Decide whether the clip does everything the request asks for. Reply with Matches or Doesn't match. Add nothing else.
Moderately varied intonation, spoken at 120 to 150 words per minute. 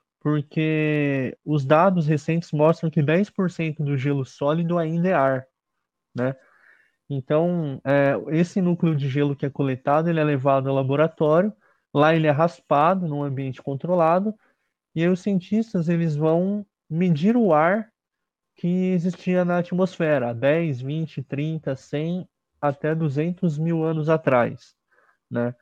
Matches